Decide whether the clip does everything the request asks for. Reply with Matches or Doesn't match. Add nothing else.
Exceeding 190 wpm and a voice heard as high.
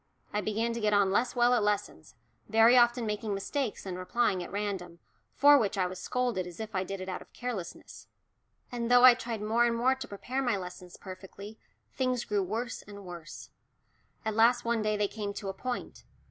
Matches